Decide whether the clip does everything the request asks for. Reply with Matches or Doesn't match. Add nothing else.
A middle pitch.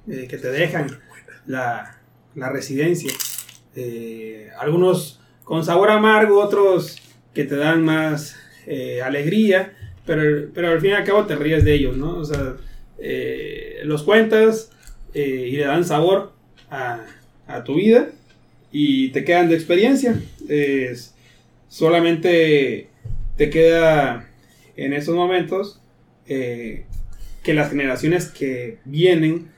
Matches